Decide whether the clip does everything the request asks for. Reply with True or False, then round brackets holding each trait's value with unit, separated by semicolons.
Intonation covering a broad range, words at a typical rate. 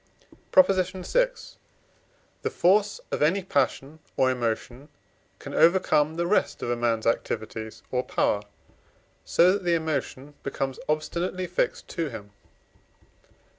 False (6.4 semitones; 125 wpm)